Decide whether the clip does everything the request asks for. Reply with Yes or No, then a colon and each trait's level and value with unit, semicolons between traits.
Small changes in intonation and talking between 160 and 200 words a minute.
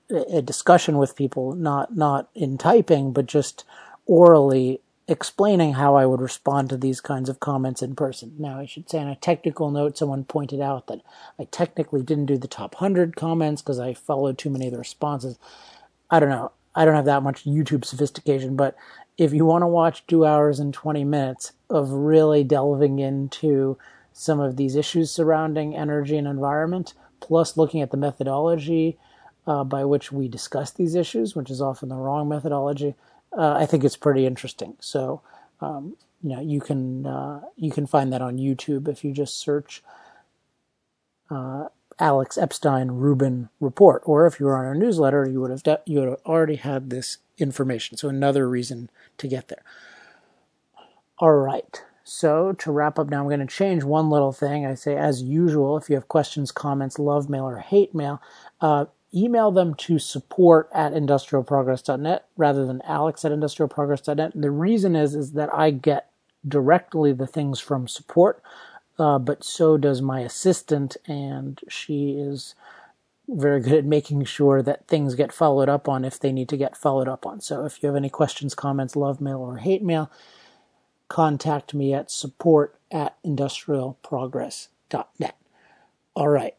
Yes: narrow, 2.3 semitones; average, 175 wpm